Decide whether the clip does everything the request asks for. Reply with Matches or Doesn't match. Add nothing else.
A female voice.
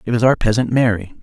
Doesn't match